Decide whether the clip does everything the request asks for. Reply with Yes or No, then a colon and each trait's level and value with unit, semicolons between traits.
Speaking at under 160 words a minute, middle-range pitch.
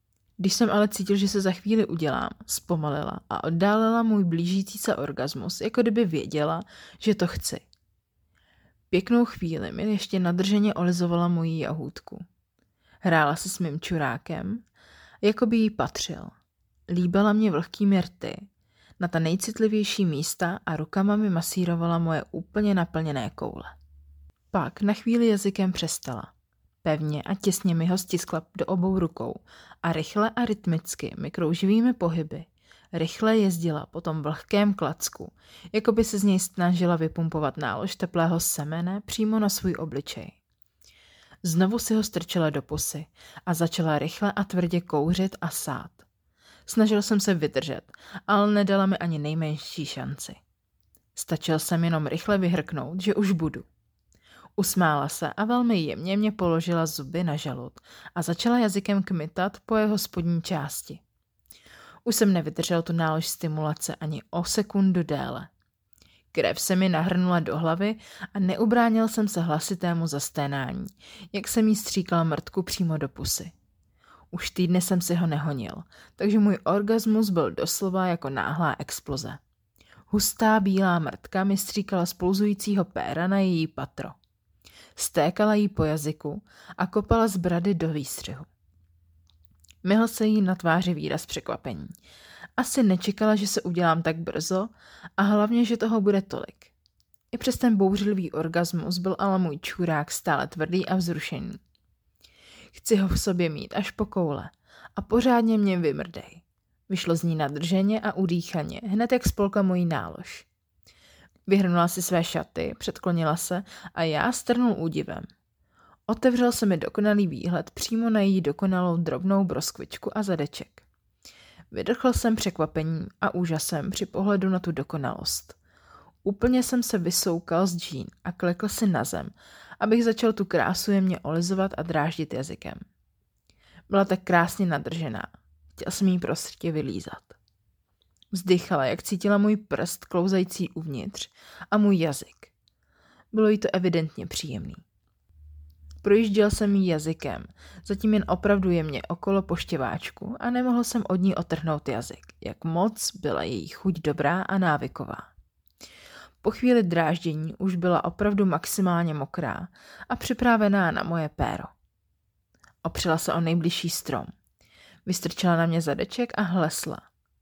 Yes: average, 140 wpm; medium, 180 Hz